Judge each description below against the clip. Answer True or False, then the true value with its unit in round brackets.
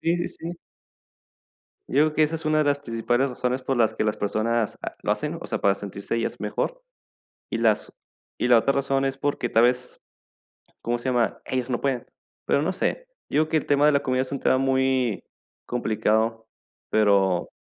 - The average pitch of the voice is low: True (130 Hz)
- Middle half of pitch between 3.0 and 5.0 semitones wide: True (3.7 semitones)